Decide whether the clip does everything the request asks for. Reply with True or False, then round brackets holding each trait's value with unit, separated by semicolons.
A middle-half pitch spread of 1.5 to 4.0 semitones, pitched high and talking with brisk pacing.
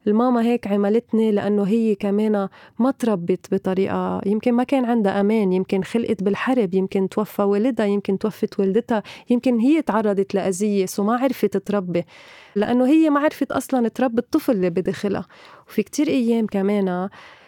True (3.5 semitones; 210 Hz; 150 wpm)